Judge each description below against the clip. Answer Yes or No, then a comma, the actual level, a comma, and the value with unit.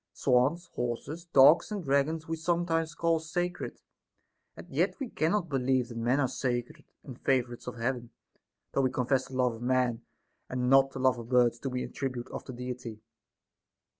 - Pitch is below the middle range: Yes, low, 130 Hz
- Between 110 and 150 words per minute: No, average, 180 wpm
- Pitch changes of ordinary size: Yes, average, 4.3 semitones